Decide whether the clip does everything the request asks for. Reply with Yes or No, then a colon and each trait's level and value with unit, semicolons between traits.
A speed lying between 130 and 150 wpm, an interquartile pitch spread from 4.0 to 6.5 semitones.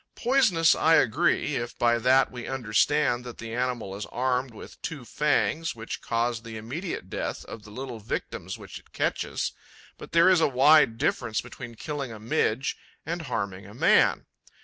No: average, 170 wpm; average, 4.7 semitones